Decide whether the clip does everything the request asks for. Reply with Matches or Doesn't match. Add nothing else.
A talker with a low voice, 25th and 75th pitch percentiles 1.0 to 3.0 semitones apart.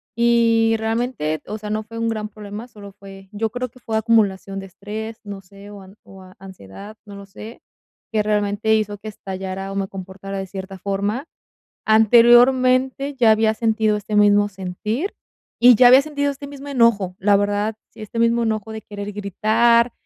Doesn't match